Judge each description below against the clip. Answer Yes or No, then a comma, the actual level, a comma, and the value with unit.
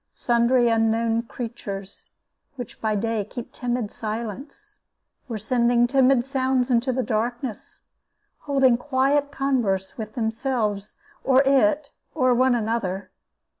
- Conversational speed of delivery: No, slow, 115 wpm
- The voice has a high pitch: Yes, high, 240 Hz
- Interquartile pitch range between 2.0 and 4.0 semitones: Yes, average, 2.9 semitones